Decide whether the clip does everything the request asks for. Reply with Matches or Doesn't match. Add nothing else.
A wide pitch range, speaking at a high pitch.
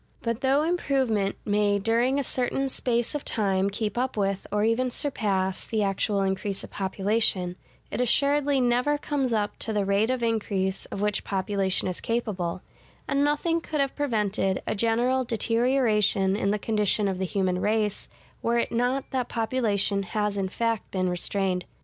Doesn't match